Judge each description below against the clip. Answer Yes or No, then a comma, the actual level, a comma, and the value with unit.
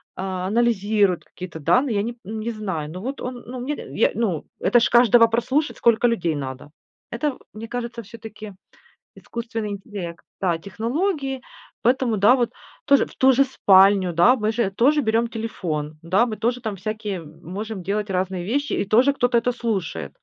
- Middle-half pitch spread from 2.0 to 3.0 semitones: No, average, 4.1 semitones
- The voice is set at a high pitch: Yes, high, 220 Hz